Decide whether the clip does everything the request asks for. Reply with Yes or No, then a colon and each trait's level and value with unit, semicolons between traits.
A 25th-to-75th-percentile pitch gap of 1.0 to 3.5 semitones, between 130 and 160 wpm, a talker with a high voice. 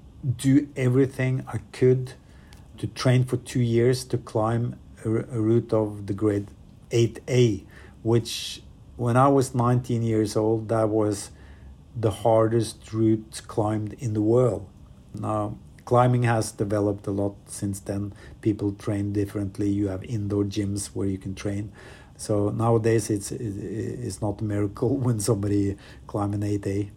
No: average, 2.7 semitones; average, 140 wpm; low, 110 Hz